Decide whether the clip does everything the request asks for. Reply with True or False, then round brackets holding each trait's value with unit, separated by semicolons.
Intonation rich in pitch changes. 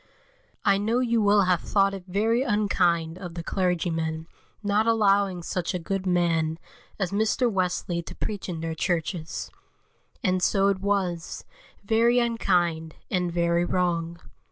False (3.0 semitones)